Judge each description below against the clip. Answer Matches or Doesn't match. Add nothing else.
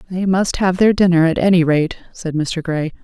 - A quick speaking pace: Matches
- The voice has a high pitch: Doesn't match